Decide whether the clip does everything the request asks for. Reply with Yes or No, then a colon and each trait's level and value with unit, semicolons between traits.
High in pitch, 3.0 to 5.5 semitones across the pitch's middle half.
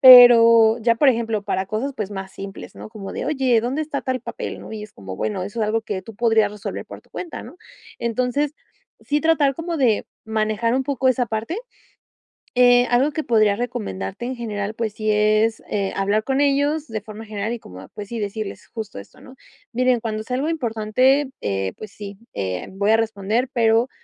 Yes: high, 225 Hz; average, 3.3 semitones